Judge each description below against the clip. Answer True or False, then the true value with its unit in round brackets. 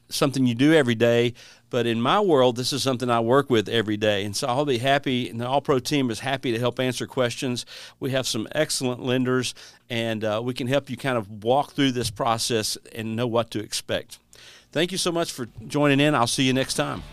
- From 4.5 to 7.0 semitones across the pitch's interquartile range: False (2.8 semitones)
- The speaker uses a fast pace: True (235 wpm)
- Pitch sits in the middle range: False (125 Hz)